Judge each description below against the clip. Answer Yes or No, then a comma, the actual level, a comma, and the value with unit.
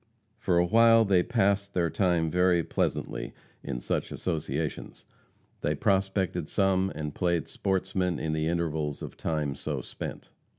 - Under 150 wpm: Yes, average, 140 wpm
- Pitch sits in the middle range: No, very low, 90 Hz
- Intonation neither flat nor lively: Yes, average, 3.4 semitones